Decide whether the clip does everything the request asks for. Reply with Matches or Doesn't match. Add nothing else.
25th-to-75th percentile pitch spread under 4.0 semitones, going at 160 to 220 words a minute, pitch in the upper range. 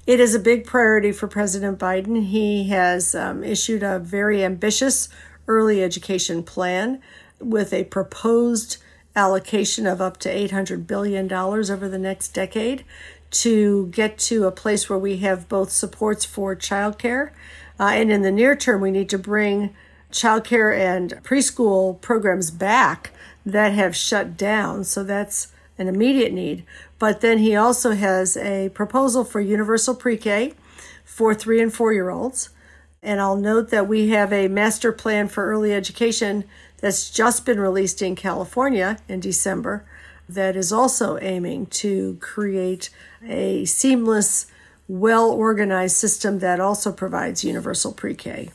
Doesn't match